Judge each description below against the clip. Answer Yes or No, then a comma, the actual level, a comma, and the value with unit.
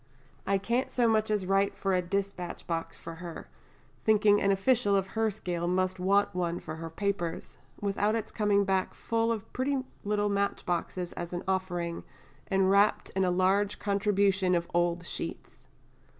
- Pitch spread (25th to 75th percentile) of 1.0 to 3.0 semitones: Yes, narrow, 2.5 semitones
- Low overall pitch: No, high, 195 Hz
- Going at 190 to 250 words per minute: No, average, 170 wpm